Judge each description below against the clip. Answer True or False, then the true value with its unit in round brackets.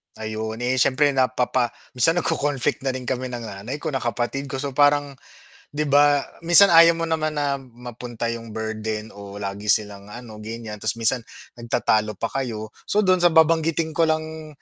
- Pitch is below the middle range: True (130 Hz)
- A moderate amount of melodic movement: True (5.0 semitones)